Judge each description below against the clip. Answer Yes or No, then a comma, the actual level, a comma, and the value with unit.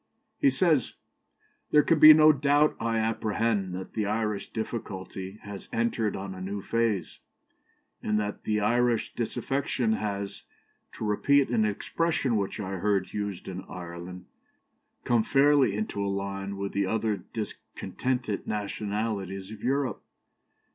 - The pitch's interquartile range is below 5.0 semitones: Yes, average, 3.4 semitones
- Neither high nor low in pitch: No, low, 105 Hz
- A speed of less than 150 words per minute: Yes, slow, 135 wpm